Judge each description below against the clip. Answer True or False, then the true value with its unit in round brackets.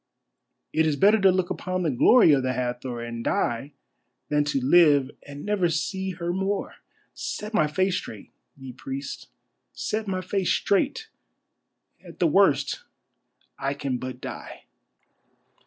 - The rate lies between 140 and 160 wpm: True (145 wpm)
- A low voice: False (155 Hz)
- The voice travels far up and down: True (6.2 semitones)